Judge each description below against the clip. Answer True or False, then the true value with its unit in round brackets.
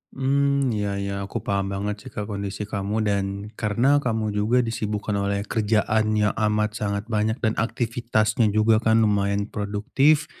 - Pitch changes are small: True (1.9 semitones)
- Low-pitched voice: True (105 Hz)